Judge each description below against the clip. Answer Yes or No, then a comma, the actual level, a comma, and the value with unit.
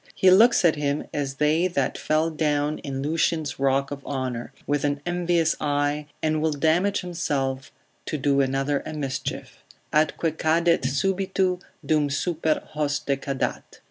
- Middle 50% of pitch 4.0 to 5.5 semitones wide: No, average, 2.9 semitones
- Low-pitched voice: No, medium, 150 Hz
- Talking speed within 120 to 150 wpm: Yes, average, 145 wpm